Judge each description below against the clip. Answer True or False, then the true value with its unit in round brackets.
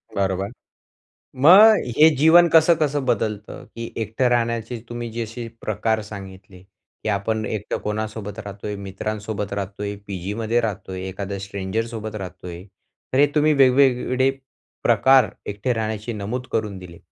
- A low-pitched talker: True (110 Hz)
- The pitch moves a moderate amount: True (3.6 semitones)